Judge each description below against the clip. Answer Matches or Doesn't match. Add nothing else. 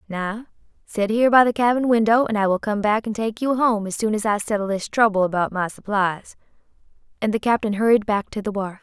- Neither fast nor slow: Doesn't match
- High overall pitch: Matches